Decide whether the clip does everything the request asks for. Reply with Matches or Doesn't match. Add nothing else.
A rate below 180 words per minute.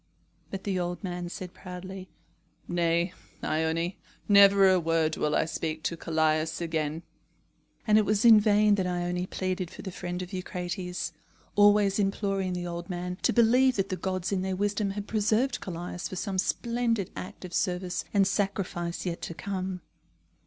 Matches